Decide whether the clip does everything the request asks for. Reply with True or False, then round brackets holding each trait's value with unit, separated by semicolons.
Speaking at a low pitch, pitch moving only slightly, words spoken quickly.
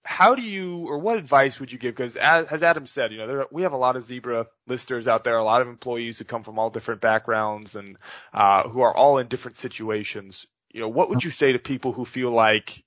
False (125 Hz; 3.4 semitones; 255 wpm)